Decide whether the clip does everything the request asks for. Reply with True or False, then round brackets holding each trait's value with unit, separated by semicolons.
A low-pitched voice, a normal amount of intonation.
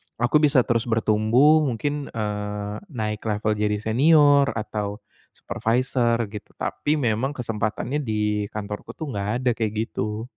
True (110 Hz; 3.9 semitones)